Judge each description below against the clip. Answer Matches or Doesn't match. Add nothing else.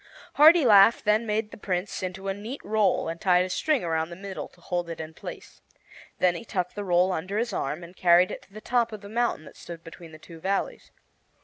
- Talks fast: Matches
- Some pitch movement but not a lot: Matches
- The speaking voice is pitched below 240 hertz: Matches